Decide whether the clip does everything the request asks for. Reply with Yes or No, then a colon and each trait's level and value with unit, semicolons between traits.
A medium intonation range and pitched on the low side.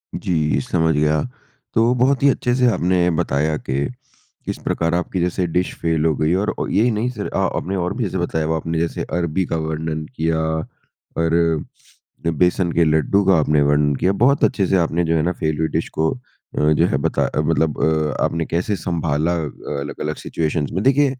Yes: average, 3.1 semitones; very low, 85 Hz